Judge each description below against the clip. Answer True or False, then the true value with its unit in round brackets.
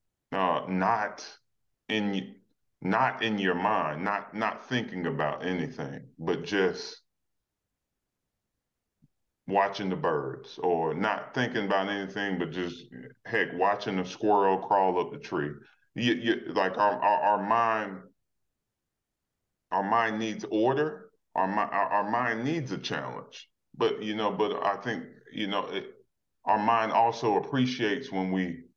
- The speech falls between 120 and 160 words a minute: True (135 wpm)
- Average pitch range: True (3.6 semitones)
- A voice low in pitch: True (105 Hz)